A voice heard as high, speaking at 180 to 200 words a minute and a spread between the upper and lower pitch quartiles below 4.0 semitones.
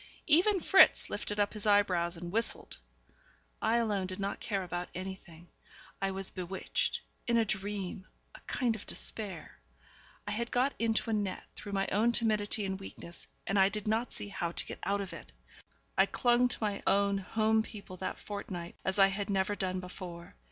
Yes: high, 200 Hz; average, 185 wpm; narrow, 2.5 semitones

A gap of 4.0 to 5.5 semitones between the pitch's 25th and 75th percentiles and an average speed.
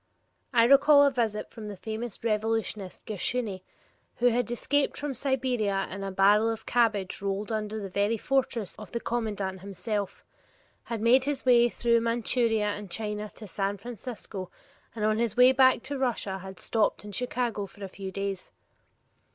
No: average, 3.1 semitones; average, 165 wpm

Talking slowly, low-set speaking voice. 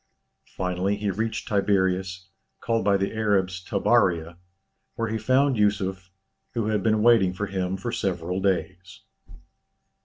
Yes: slow, 130 wpm; very low, 95 Hz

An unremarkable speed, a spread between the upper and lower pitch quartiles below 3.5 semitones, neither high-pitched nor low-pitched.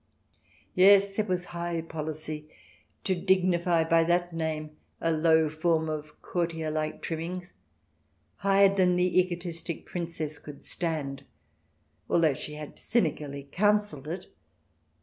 No: slow, 120 wpm; average, 2.7 semitones; medium, 165 Hz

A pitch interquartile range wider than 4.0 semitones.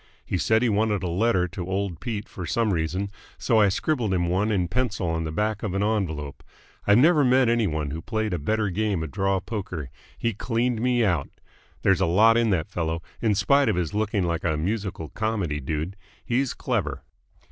Yes: average, 4.4 semitones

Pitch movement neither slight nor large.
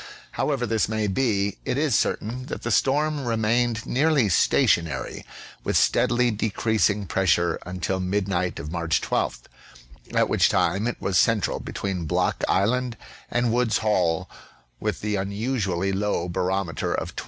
Yes: average, 4.4 semitones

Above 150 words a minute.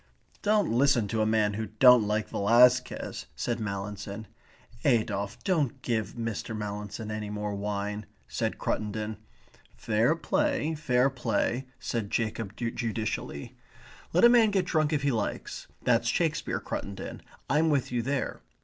No: average, 140 wpm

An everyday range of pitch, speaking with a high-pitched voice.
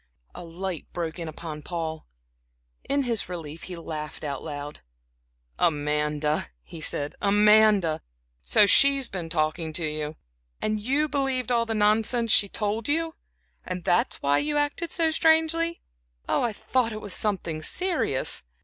No: wide, 8.1 semitones; high, 195 Hz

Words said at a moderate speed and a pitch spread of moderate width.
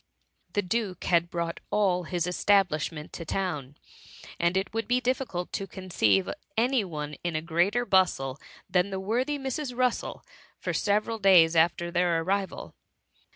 Yes: average, 150 wpm; average, 3.8 semitones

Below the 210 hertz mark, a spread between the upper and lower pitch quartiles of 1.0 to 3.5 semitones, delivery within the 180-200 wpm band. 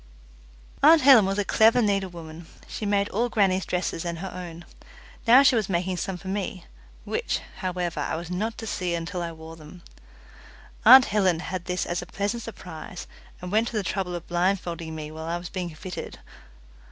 Yes: medium, 185 Hz; average, 3.1 semitones; average, 190 wpm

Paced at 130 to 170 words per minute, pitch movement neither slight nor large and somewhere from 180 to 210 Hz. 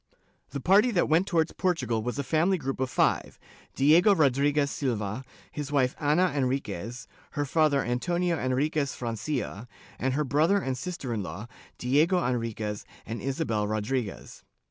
No: average, 150 wpm; average, 4.5 semitones; low, 135 Hz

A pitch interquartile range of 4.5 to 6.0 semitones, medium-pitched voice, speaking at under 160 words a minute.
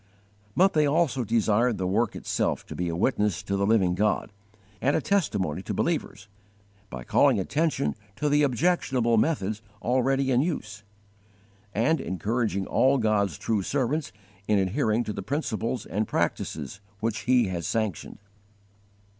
No: average, 5.2 semitones; low, 110 Hz; average, 145 wpm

